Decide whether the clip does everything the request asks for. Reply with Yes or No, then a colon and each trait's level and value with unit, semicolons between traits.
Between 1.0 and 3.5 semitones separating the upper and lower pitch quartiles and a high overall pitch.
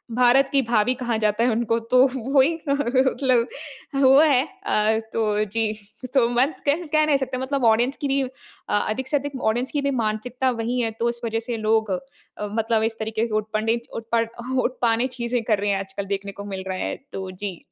Yes: average, 3.2 semitones; high, 235 Hz